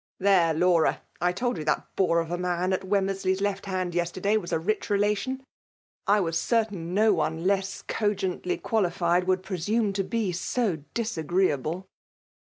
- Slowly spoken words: No, average, 175 wpm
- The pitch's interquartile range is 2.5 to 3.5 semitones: Yes, average, 2.8 semitones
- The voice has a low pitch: No, medium, 185 Hz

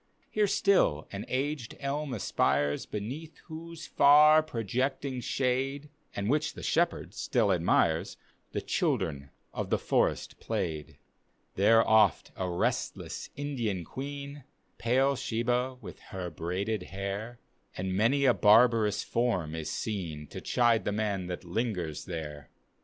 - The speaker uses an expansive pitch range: Yes, wide, 6.7 semitones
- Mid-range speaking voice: No, low, 115 Hz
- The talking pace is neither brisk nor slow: No, slow, 130 wpm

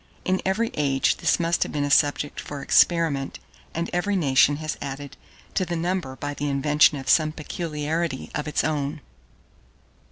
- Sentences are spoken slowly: No, average, 165 wpm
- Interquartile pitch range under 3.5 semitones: Yes, average, 2.9 semitones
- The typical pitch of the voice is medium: Yes, medium, 150 Hz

